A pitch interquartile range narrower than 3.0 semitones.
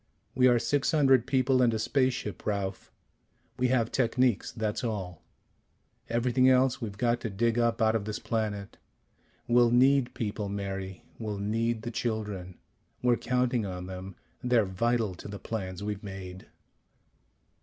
No: average, 3.5 semitones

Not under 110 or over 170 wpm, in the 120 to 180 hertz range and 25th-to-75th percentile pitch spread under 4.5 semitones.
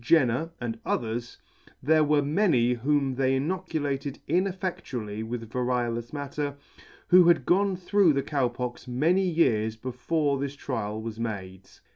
No: slow, 135 wpm; low, 135 Hz; average, 5.1 semitones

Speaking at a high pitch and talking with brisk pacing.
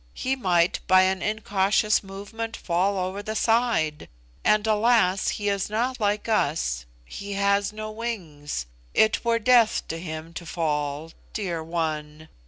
No: high, 200 Hz; average, 145 wpm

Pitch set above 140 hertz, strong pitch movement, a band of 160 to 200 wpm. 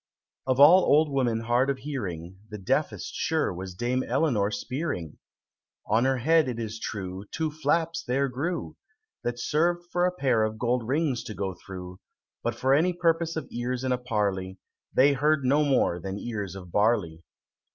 No: low, 125 Hz; wide, 6.1 semitones; average, 180 wpm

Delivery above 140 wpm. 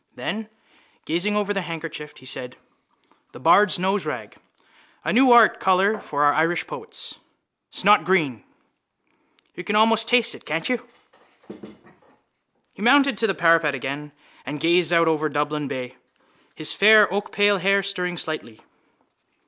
No: slow, 135 wpm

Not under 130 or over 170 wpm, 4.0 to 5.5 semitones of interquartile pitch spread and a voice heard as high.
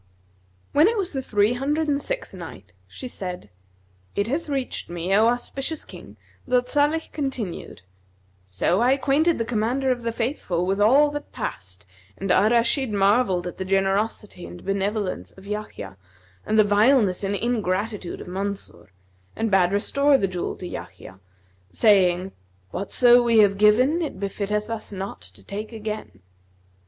Yes: average, 160 wpm; average, 4.8 semitones; high, 215 Hz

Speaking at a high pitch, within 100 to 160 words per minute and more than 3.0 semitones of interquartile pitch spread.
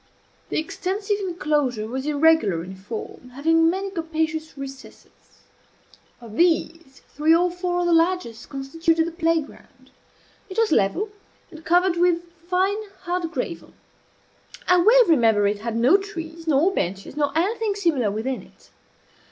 Yes: very high, 325 Hz; average, 145 wpm; average, 4.9 semitones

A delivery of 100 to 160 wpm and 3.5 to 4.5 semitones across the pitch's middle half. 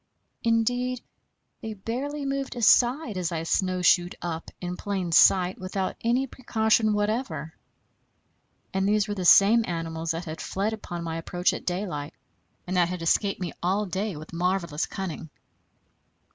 Yes: average, 145 wpm; average, 4.2 semitones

